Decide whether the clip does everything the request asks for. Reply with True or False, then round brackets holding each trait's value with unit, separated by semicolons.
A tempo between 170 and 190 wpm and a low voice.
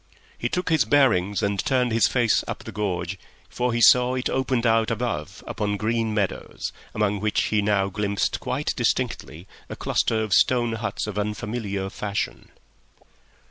False (160 wpm; 105 Hz)